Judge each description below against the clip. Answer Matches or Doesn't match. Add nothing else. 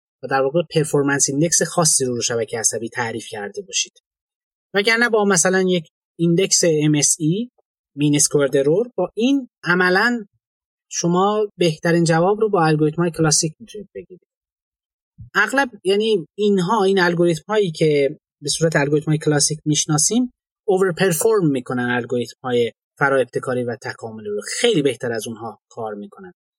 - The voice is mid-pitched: Matches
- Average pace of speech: Matches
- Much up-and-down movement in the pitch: Matches